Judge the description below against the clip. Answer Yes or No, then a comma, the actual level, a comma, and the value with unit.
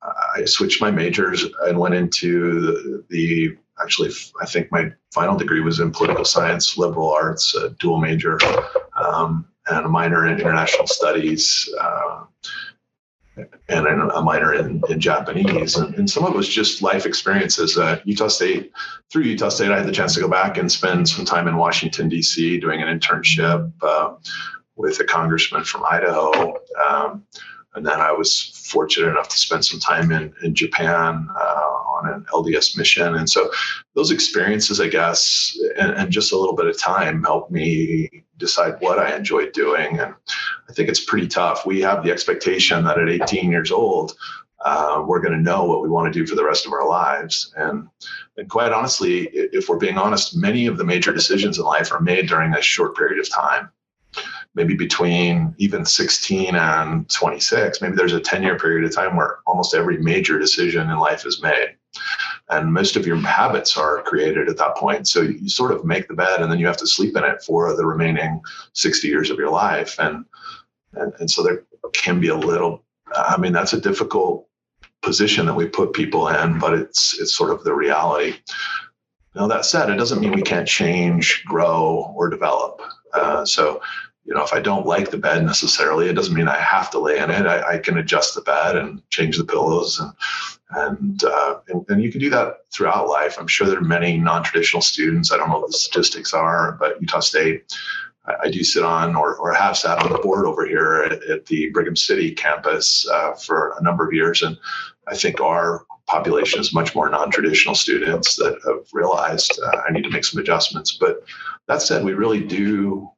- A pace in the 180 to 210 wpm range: Yes, average, 200 wpm